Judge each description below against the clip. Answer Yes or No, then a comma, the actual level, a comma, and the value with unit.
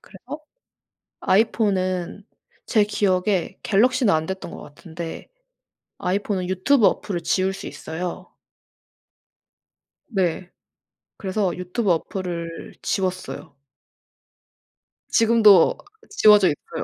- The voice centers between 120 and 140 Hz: No, high, 190 Hz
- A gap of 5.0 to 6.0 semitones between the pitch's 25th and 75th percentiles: No, average, 2.7 semitones